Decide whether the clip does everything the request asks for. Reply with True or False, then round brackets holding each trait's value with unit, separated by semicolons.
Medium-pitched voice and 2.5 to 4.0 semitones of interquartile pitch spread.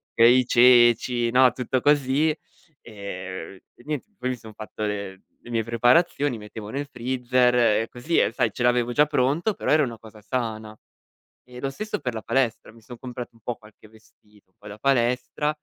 False (120 Hz; 2.8 semitones)